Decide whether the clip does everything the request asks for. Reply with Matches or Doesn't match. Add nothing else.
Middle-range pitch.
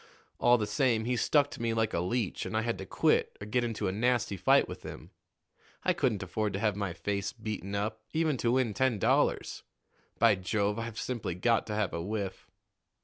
Doesn't match